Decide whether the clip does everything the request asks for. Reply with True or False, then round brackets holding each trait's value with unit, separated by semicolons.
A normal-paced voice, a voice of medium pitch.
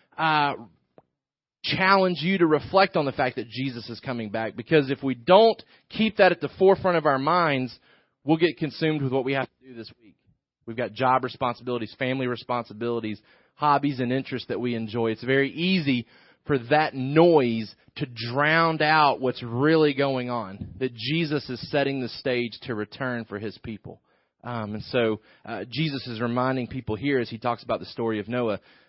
False (185 wpm; 130 Hz)